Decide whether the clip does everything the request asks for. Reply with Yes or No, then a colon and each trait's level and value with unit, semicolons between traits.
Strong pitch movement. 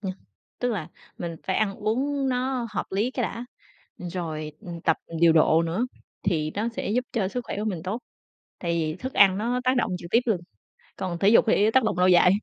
Yes: wide, 5.7 semitones